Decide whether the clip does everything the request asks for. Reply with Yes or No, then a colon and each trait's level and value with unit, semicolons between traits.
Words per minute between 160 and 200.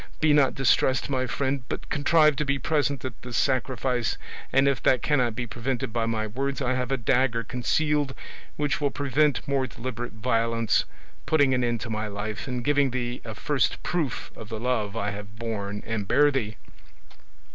Yes: average, 185 wpm